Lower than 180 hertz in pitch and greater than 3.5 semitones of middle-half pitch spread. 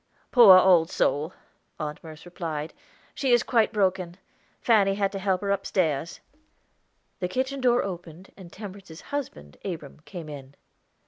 No: medium, 185 Hz; average, 4.0 semitones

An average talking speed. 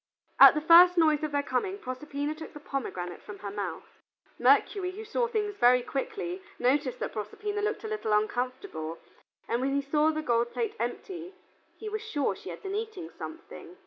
Yes: average, 185 wpm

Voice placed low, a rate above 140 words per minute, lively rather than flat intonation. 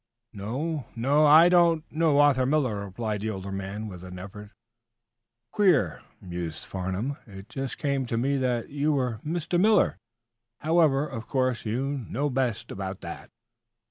Yes: low, 130 Hz; average, 155 wpm; wide, 6.4 semitones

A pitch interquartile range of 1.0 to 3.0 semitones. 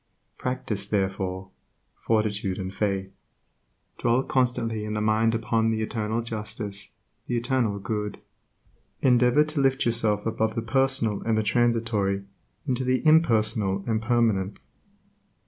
Yes: average, 2.7 semitones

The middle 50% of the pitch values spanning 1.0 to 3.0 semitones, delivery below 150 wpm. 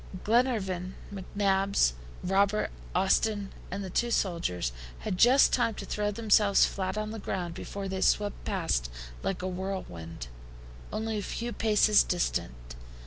Yes: average, 2.7 semitones; average, 140 wpm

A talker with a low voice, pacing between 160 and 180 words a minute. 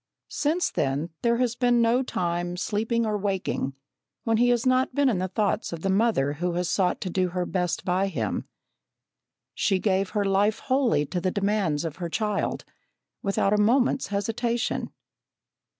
No: high, 200 Hz; average, 170 wpm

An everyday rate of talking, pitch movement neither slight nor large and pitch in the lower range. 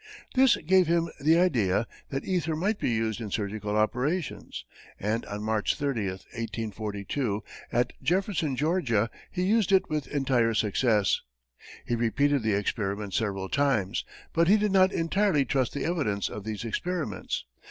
No: average, 150 wpm; wide, 7.7 semitones; low, 125 Hz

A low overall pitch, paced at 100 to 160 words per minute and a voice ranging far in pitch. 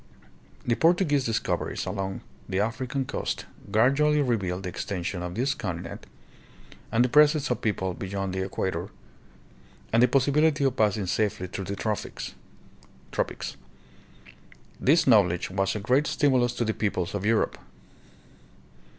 Yes: low, 110 Hz; average, 140 wpm; wide, 5.7 semitones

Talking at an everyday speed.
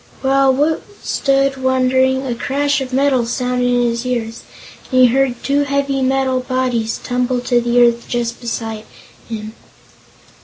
Yes: average, 145 wpm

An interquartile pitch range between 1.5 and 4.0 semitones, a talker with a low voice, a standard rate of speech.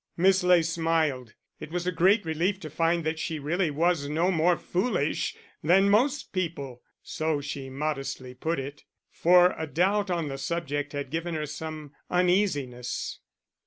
No: average, 3.6 semitones; medium, 160 Hz; average, 160 wpm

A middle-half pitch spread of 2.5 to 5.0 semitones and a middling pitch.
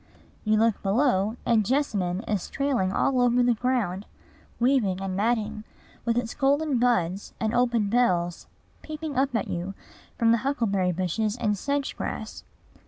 No: average, 4.2 semitones; high, 230 Hz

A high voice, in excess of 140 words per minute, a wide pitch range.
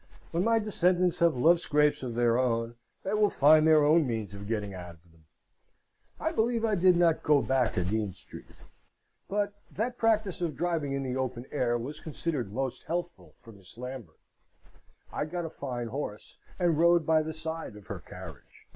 No: medium, 150 Hz; average, 190 wpm; wide, 6.5 semitones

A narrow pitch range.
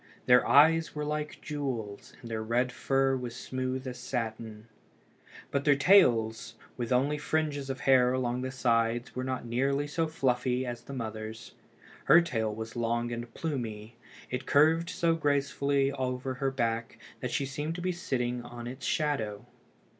No: average, 3.2 semitones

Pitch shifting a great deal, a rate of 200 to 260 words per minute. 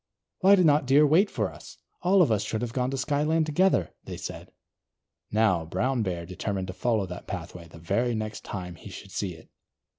Yes: wide, 7.9 semitones; fast, 205 wpm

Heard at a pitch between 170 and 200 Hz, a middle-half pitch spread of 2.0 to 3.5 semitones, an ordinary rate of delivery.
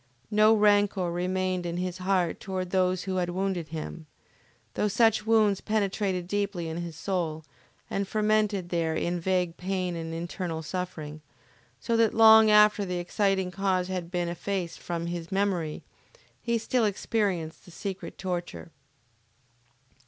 Yes: medium, 185 Hz; average, 2.8 semitones; average, 145 wpm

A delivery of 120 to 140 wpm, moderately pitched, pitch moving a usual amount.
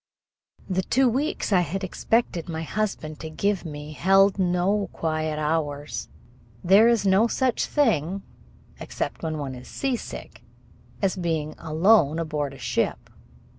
Yes: slow, 135 wpm; medium, 175 Hz; average, 4.7 semitones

